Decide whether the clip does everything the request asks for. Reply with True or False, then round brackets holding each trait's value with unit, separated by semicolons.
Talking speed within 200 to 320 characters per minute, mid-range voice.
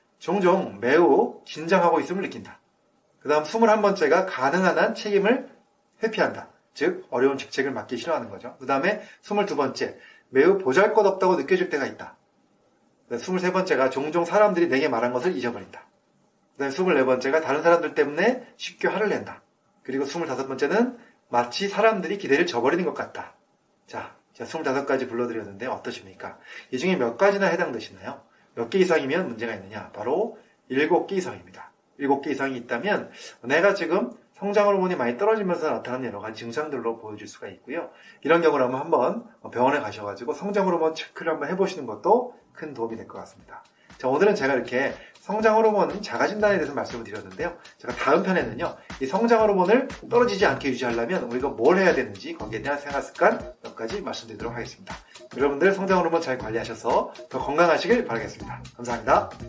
False (390 characters per minute; 160 Hz)